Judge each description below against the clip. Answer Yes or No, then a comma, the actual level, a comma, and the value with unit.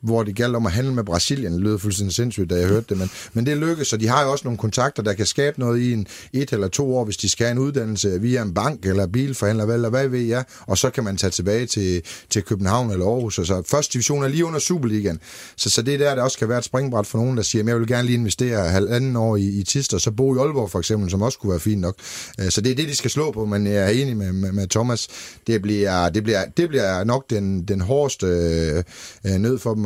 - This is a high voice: No, low, 110 Hz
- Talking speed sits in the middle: No, fast, 285 wpm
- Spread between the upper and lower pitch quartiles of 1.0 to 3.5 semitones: No, average, 4.2 semitones